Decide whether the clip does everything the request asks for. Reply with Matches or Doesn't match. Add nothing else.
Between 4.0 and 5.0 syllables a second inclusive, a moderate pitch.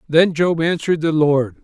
Matches